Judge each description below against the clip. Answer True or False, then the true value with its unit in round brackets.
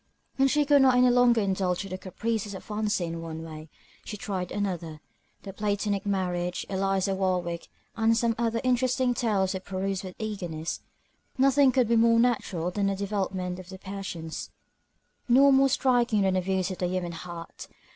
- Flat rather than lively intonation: False (4.2 semitones)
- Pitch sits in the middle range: False (195 Hz)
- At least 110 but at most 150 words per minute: False (170 wpm)